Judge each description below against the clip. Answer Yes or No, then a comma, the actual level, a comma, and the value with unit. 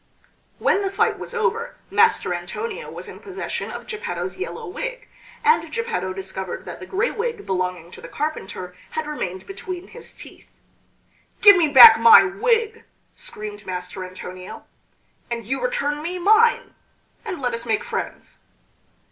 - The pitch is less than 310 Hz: No, very high, 375 Hz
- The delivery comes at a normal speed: Yes, average, 150 wpm